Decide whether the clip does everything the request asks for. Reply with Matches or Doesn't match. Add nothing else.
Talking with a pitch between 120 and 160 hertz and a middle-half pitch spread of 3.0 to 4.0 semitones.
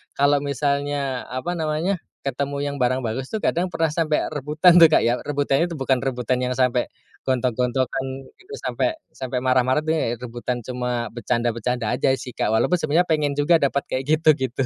Matches